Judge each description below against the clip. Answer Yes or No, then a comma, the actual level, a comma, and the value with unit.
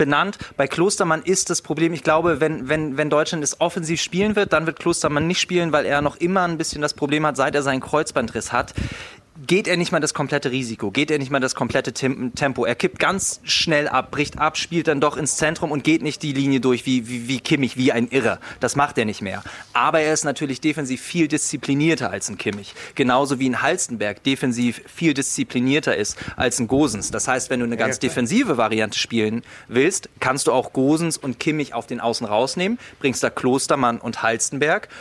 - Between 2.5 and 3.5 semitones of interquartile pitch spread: No, average, 3.9 semitones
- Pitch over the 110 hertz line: Yes, medium, 140 Hz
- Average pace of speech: No, fast, 215 wpm